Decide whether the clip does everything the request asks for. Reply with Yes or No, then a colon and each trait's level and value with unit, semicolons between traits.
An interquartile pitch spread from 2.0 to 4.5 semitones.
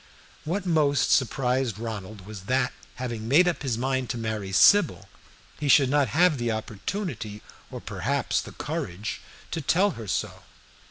No: average, 5.2 semitones